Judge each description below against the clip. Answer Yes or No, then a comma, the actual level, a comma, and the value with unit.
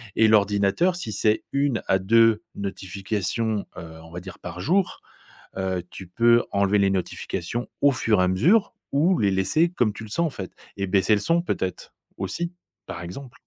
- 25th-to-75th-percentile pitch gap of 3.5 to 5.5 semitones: Yes, average, 5.1 semitones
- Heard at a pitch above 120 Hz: No, low, 105 Hz